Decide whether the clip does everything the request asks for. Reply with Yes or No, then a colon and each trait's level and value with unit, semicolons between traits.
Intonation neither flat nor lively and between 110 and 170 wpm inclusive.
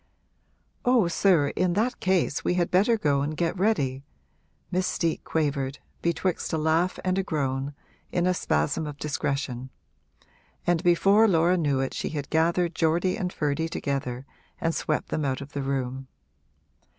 Yes: average, 4.4 semitones; average, 160 wpm